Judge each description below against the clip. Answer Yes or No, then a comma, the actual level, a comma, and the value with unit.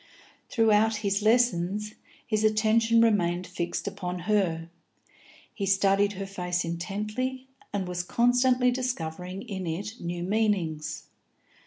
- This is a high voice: Yes, high, 200 Hz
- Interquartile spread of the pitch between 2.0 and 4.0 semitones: Yes, average, 3.7 semitones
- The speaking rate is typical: No, slow, 115 wpm